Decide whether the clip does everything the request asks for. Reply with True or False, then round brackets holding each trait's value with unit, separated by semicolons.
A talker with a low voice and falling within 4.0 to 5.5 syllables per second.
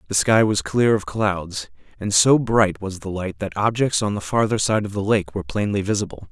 True (100 Hz; 5.2 syllables/s)